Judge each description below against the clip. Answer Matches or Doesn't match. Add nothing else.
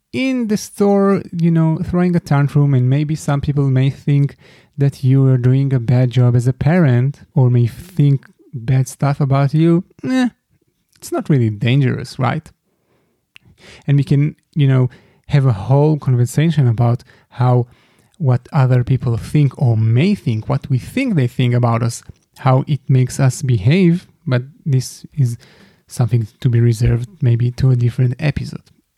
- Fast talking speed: Doesn't match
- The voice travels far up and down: Doesn't match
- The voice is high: Doesn't match